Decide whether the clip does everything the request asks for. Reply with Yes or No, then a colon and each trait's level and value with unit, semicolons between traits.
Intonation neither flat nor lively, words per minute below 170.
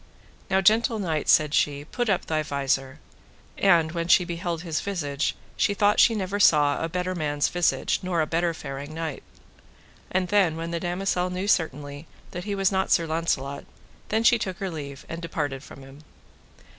No: average, 4.1 semitones; average, 180 wpm